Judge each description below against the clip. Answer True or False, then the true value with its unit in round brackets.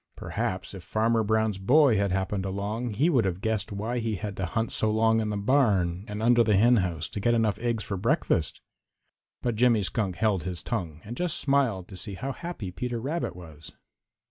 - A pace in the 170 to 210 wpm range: True (200 wpm)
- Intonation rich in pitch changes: False (3.5 semitones)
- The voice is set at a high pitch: False (110 Hz)